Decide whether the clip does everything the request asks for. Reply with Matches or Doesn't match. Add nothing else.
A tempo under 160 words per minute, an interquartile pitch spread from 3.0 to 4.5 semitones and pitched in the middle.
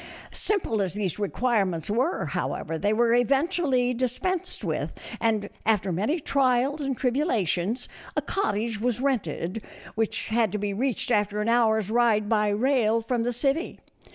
Doesn't match